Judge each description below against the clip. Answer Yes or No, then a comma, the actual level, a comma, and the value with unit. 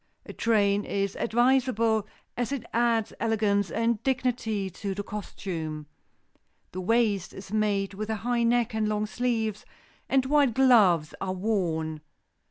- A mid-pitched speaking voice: No, high, 215 Hz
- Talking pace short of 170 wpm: Yes, average, 140 wpm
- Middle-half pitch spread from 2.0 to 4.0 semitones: Yes, average, 3.1 semitones